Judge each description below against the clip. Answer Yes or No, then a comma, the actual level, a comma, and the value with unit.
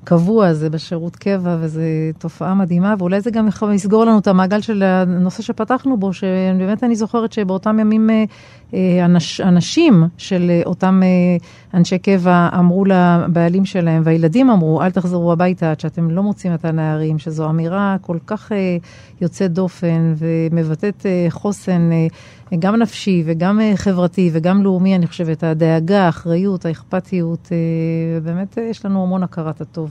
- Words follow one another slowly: No, average, 135 wpm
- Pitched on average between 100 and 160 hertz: No, medium, 180 Hz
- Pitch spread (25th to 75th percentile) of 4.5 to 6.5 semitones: No, average, 3.0 semitones